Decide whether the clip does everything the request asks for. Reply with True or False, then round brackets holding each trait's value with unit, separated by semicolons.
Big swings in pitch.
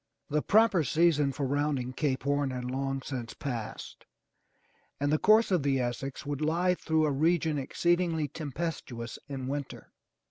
False (3.3 semitones)